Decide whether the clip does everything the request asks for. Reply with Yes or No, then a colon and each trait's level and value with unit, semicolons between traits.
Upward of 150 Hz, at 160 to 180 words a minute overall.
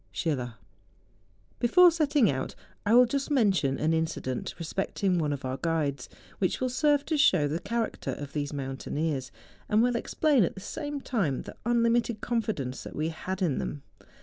Yes: medium, 185 Hz; average, 175 wpm